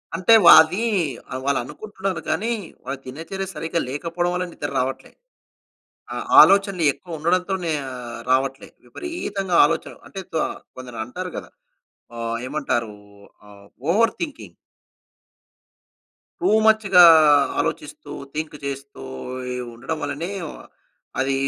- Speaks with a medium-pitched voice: Yes, medium, 160 Hz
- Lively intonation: Yes, wide, 5.9 semitones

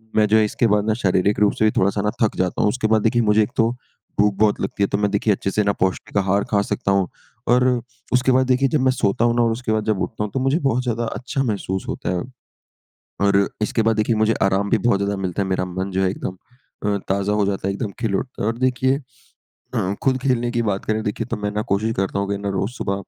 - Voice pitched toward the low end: Yes, low, 105 Hz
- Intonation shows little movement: No, average, 3.0 semitones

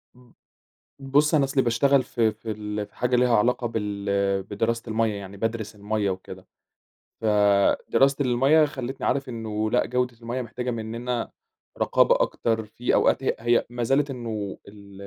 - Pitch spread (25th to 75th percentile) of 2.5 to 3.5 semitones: Yes, average, 3.0 semitones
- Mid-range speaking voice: No, low, 115 Hz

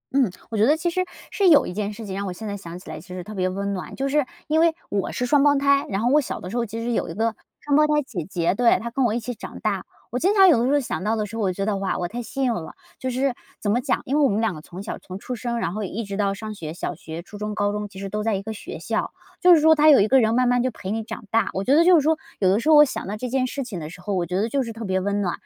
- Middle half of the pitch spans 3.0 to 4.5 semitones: No, average, 5.3 semitones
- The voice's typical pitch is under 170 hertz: No, high, 220 Hz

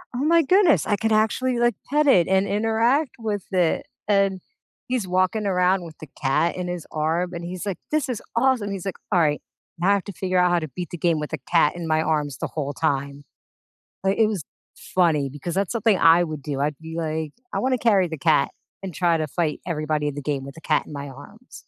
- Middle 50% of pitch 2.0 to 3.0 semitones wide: No, average, 5.1 semitones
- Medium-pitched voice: Yes, medium, 175 Hz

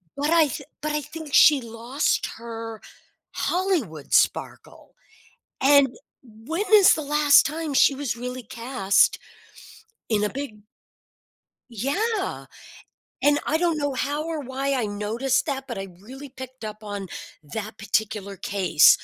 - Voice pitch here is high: Yes, very high, 260 Hz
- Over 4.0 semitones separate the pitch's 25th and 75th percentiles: Yes, average, 5.0 semitones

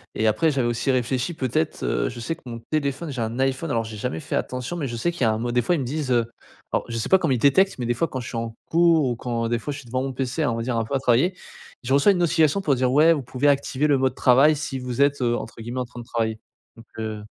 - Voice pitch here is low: Yes, low, 130 Hz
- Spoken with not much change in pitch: No, average, 3.7 semitones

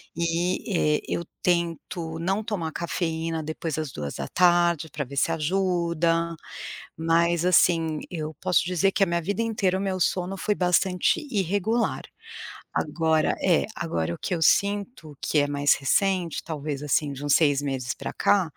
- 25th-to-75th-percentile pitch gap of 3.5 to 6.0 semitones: No, average, 2.9 semitones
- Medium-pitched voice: Yes, medium, 170 Hz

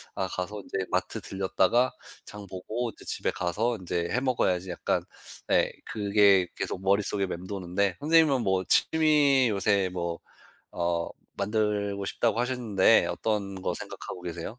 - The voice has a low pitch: Yes, low, 100 Hz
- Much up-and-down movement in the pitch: No, average, 3.6 semitones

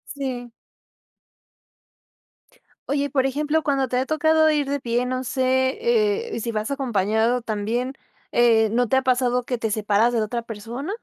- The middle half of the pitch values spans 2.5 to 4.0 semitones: Yes, average, 3.4 semitones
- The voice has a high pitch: Yes, very high, 250 Hz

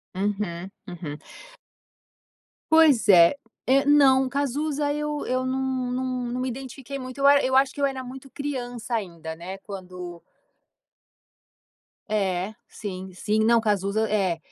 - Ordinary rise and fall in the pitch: No, wide, 5.8 semitones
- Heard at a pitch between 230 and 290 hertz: Yes, high, 245 Hz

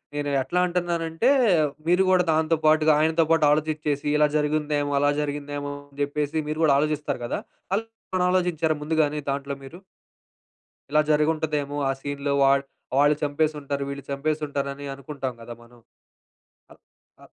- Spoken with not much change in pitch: Yes, narrow, 1.8 semitones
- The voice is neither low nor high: Yes, medium, 150 Hz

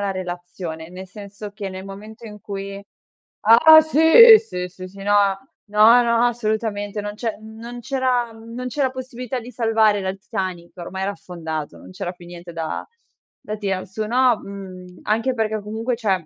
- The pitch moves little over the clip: No, average, 3.7 semitones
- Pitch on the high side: Yes, high, 210 Hz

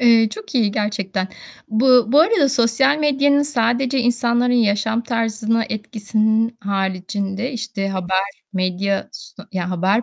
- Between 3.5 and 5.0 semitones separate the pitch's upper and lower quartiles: Yes, average, 3.8 semitones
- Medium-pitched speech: No, high, 225 Hz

